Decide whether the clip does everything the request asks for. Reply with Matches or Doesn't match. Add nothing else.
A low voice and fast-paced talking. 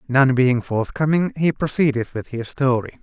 Doesn't match